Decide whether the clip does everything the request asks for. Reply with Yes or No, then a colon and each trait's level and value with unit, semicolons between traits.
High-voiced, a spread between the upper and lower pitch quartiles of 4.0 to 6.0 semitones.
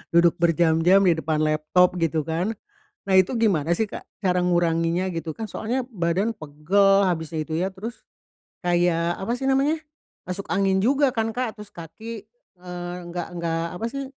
No: medium, 180 Hz; average, 4.5 semitones